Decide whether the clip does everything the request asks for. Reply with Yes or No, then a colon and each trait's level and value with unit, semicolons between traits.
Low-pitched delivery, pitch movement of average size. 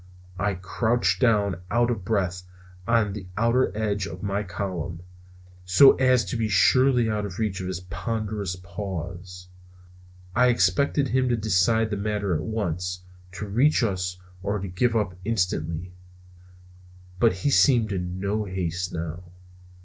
Yes: low, 100 Hz; average, 3.8 semitones